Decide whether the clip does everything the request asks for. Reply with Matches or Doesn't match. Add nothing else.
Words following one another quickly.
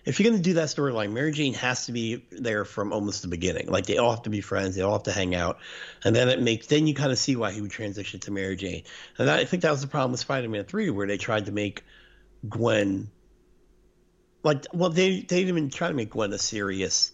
Matches